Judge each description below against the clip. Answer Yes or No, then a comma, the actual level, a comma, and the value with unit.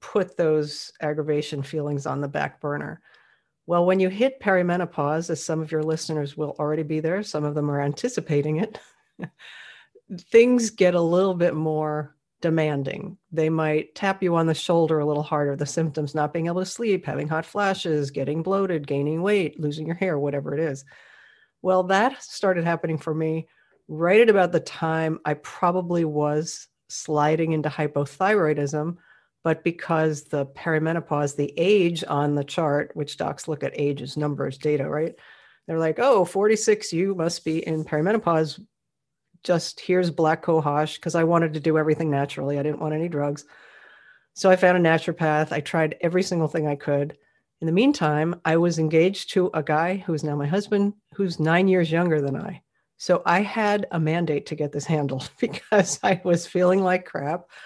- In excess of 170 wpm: Yes, average, 180 wpm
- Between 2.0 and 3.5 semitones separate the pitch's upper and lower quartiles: Yes, average, 3.2 semitones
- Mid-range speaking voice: Yes, medium, 160 Hz